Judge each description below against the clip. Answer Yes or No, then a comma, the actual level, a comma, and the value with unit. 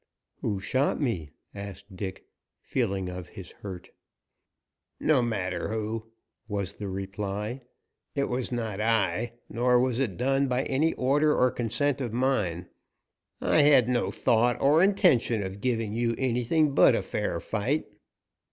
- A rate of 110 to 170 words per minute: Yes, average, 145 wpm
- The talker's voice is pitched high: No, low, 115 Hz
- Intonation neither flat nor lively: Yes, average, 4.6 semitones